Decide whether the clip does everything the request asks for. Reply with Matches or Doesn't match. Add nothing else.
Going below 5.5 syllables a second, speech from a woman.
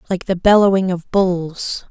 Matches